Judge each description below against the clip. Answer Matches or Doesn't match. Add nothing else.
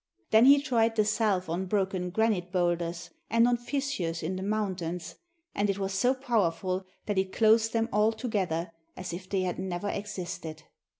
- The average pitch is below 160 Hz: Doesn't match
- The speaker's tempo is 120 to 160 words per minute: Doesn't match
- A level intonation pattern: Doesn't match